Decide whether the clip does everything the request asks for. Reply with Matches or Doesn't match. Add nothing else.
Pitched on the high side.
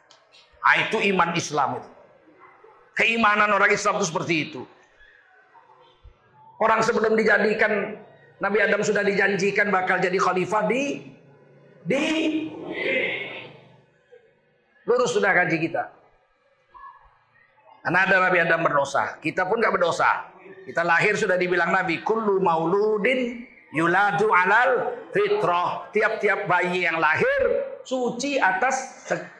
Matches